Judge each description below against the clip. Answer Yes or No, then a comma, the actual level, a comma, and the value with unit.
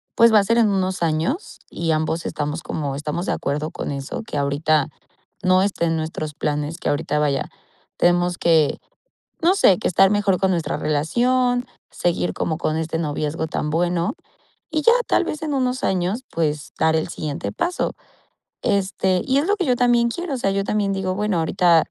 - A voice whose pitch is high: No, medium, 175 Hz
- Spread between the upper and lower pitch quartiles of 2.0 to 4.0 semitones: No, average, 5.2 semitones